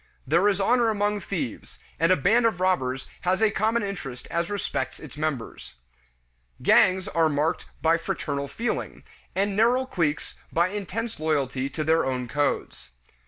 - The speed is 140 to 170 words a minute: Yes, average, 155 wpm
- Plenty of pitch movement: Yes, wide, 6.1 semitones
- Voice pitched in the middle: Yes, medium, 170 Hz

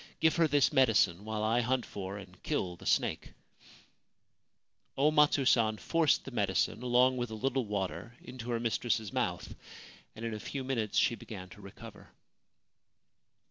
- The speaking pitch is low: Yes, low, 115 Hz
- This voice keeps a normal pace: Yes, average, 160 wpm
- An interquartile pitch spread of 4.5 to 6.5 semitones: No, average, 3.8 semitones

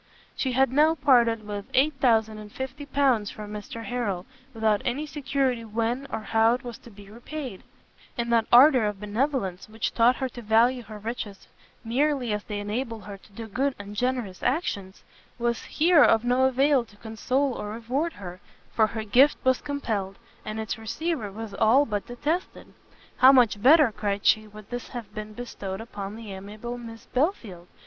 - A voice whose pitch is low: No, high, 230 Hz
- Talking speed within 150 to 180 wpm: Yes, average, 175 wpm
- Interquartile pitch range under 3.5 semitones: No, average, 3.8 semitones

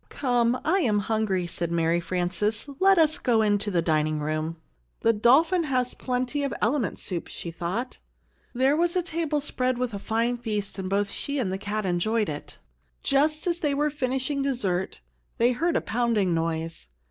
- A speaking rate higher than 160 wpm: Yes, average, 180 wpm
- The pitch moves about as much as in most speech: No, wide, 7.0 semitones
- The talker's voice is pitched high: Yes, high, 230 Hz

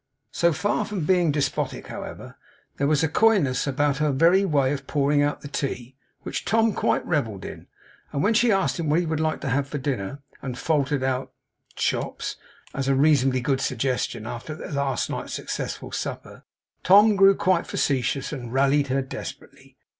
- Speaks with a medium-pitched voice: Yes, medium, 145 Hz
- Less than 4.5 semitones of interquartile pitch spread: Yes, average, 3.8 semitones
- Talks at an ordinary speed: Yes, average, 180 wpm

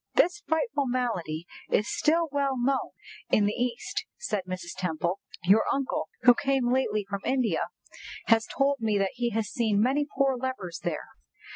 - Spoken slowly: No, average, 160 wpm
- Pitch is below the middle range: No, high, 240 Hz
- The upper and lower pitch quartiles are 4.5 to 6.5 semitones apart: Yes, average, 5.3 semitones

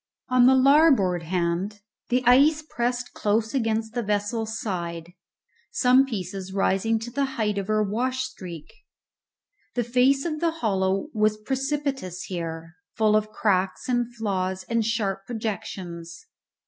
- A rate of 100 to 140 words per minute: Yes, slow, 135 wpm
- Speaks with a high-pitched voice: Yes, high, 220 Hz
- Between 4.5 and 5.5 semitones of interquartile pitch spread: Yes, average, 4.9 semitones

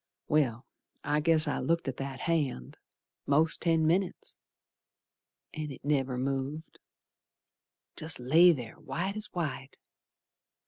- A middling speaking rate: No, slow, 120 wpm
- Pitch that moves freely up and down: No, average, 3.5 semitones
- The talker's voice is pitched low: No, medium, 150 Hz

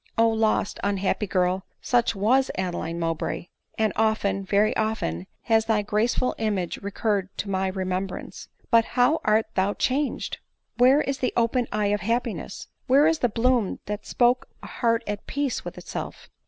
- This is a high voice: Yes, high, 215 Hz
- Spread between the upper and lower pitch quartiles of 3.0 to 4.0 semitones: Yes, average, 3.7 semitones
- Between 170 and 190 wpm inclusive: No, average, 160 wpm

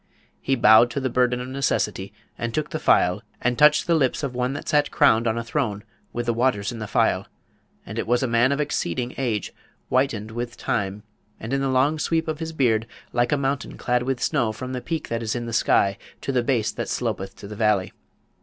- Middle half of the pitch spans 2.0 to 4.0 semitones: Yes, average, 3.3 semitones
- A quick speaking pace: Yes, fast, 230 wpm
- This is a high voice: No, low, 125 Hz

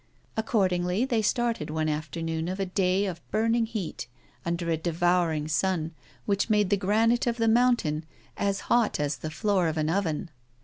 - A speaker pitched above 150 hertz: Yes, medium, 185 Hz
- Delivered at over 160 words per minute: Yes, average, 170 wpm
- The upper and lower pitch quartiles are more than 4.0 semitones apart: Yes, average, 5.0 semitones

